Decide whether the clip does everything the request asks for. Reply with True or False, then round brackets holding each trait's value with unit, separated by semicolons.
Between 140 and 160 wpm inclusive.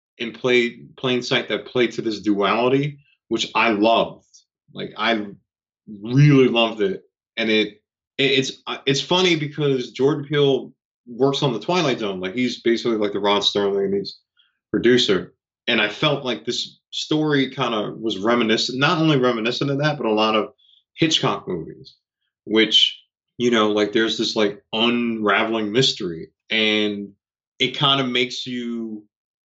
True (155 wpm)